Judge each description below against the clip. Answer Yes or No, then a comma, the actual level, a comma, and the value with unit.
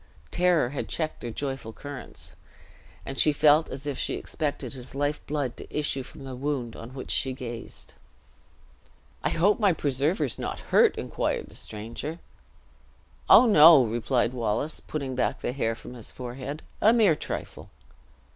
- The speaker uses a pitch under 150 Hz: Yes, medium, 140 Hz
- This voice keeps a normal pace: Yes, average, 160 wpm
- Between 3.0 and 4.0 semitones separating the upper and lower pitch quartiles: Yes, average, 3.5 semitones